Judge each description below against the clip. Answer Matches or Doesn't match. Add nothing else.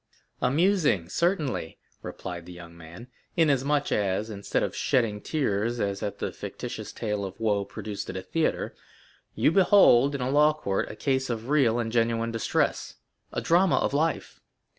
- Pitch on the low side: Matches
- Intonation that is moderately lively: Doesn't match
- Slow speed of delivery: Doesn't match